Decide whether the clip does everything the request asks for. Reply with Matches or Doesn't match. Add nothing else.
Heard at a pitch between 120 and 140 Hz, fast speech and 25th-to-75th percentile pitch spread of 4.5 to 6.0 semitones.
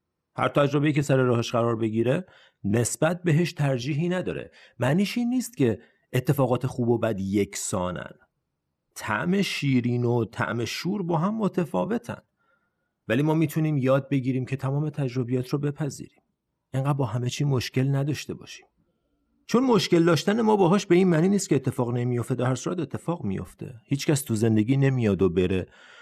Matches